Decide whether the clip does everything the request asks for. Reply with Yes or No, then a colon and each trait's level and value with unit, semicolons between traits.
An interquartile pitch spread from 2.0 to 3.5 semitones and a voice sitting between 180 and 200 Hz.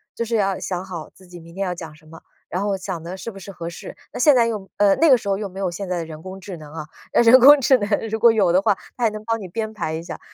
No: average, 4.3 semitones; high, 195 Hz